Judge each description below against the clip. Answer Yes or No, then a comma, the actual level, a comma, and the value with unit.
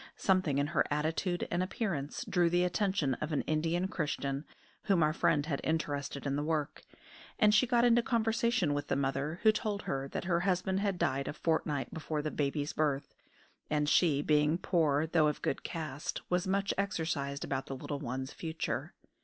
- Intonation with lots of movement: No, average, 4.3 semitones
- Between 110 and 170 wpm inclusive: No, average, 185 wpm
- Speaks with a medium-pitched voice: Yes, medium, 155 Hz